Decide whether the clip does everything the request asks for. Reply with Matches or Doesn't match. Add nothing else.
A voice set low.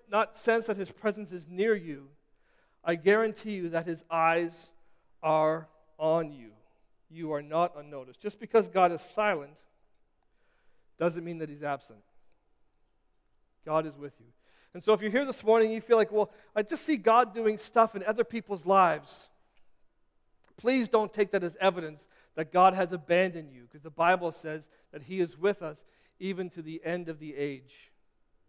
Doesn't match